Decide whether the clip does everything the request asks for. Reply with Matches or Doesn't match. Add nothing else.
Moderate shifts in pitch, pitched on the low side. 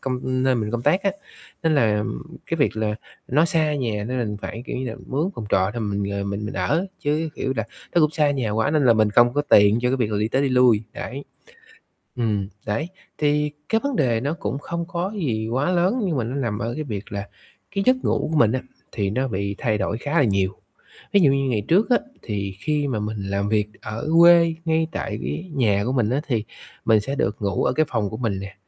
Doesn't match